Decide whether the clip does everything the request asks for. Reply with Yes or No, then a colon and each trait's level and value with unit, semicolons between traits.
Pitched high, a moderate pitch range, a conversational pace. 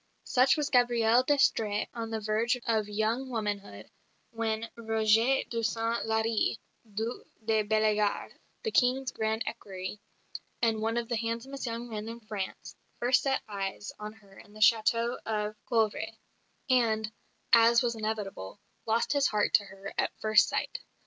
No: high, 225 Hz; narrow, 1.8 semitones; average, 150 wpm